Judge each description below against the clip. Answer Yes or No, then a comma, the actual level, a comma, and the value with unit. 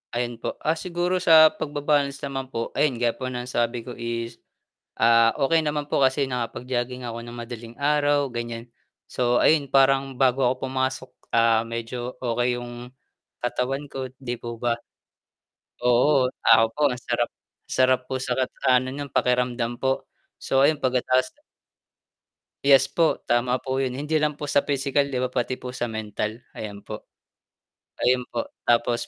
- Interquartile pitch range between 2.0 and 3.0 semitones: Yes, narrow, 2.4 semitones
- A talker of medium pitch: No, low, 125 Hz